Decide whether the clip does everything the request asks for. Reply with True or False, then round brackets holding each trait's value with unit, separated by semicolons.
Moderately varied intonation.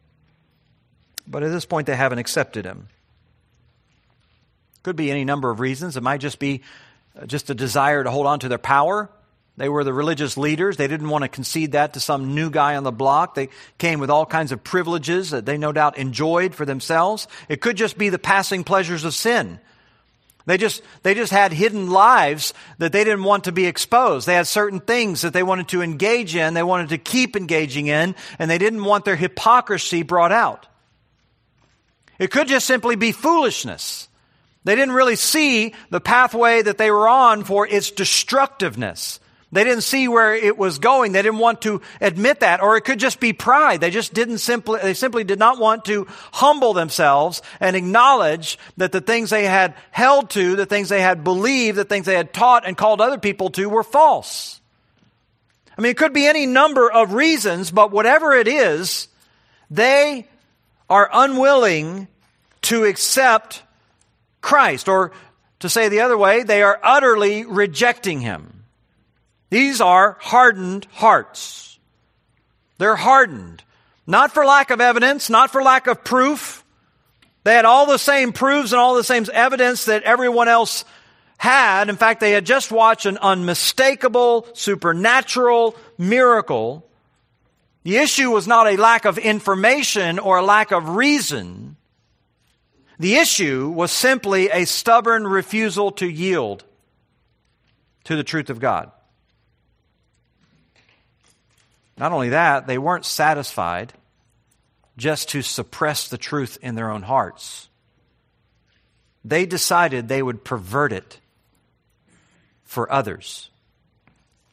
False (7.3 semitones)